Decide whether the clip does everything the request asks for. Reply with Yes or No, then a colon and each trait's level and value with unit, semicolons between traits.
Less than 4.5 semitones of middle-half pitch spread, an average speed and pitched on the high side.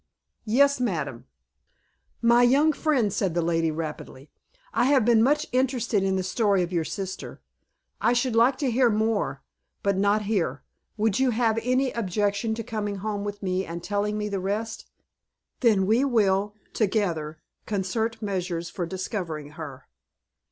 Yes: average, 4.0 semitones; average, 155 wpm; high, 210 Hz